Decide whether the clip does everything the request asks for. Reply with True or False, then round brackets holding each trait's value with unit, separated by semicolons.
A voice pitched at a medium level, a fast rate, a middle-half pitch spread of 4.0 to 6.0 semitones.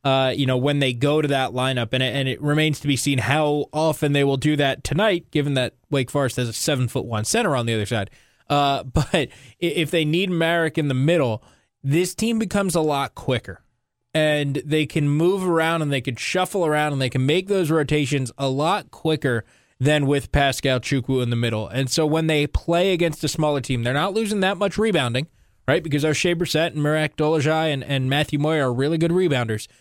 False (145 Hz; 220 wpm; 3.5 semitones)